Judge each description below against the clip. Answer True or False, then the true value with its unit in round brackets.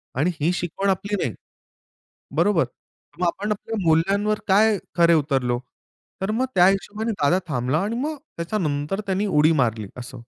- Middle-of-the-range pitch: True (180 Hz)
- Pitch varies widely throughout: True (5.7 semitones)